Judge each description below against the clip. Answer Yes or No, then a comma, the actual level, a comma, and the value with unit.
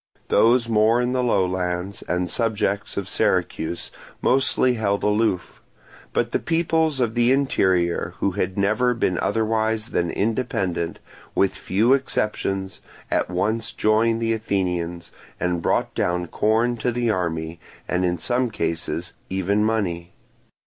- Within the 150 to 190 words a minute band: No, slow, 135 wpm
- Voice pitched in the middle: No, low, 105 Hz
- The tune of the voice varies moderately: Yes, average, 4.3 semitones